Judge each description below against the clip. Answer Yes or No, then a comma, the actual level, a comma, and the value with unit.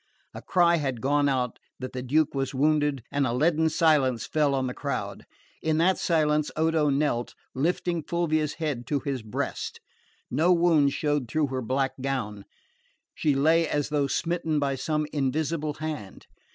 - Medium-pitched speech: Yes, medium, 145 Hz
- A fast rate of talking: No, average, 165 wpm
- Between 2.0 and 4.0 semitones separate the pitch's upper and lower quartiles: Yes, average, 2.8 semitones